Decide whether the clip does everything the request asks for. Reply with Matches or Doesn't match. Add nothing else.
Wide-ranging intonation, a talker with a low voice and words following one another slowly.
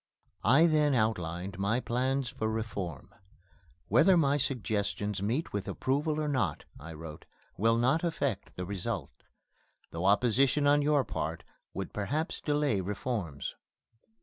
Matches